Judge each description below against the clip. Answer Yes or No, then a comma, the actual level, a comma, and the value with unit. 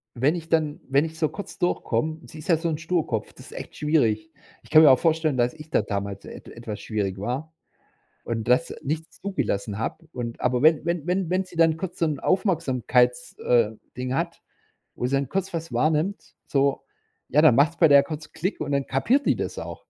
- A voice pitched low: No, medium, 150 Hz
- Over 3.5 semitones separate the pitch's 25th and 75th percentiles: Yes, average, 4.8 semitones